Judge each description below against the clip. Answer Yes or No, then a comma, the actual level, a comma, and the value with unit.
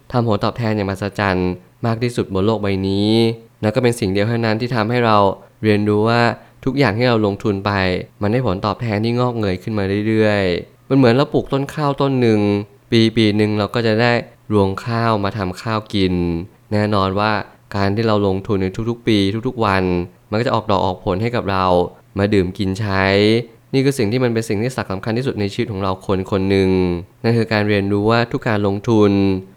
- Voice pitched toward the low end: Yes, low, 105 Hz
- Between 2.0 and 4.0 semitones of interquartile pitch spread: Yes, average, 3.1 semitones